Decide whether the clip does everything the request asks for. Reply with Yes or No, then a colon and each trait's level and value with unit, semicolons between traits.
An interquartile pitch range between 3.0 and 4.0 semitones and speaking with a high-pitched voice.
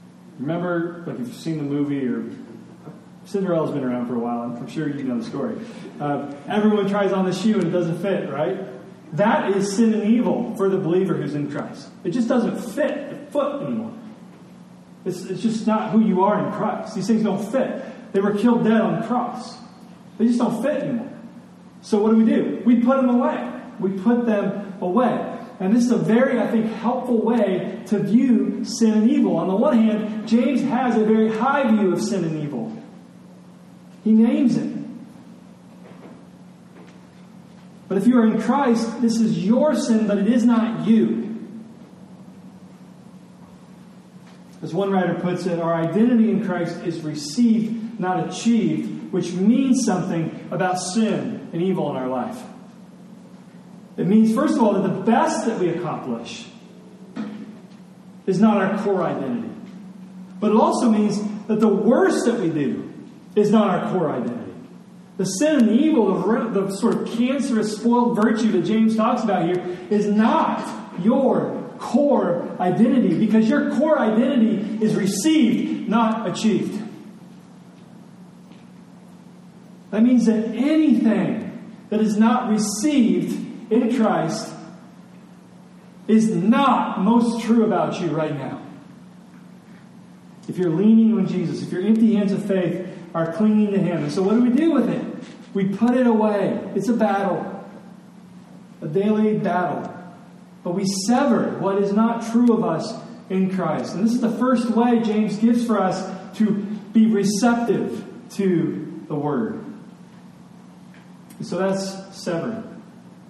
Yes: average, 3.5 semitones; high, 210 Hz